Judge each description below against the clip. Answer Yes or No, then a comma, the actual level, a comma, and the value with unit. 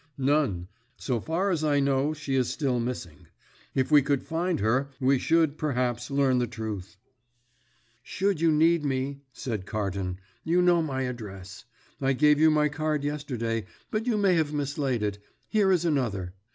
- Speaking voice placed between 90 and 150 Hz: Yes, medium, 140 Hz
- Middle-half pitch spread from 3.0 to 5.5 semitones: Yes, average, 4.7 semitones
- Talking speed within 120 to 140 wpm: No, average, 165 wpm